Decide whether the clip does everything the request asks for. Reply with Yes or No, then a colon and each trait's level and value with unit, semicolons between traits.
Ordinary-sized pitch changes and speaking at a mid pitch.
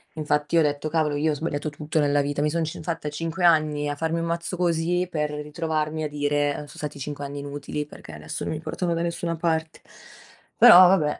No: narrow, 2.2 semitones; medium, 155 Hz